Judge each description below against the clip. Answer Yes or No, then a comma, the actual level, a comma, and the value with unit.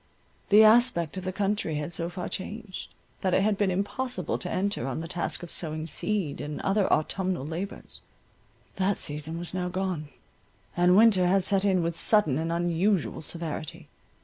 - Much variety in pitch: No, average, 3.2 semitones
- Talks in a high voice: No, medium, 180 Hz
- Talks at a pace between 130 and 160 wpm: No, average, 175 wpm